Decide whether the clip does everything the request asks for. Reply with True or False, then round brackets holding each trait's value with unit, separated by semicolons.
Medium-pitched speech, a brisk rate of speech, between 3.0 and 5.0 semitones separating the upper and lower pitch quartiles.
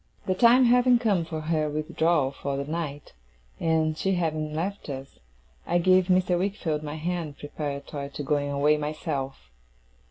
False (155 Hz; 155 wpm; 3.5 semitones)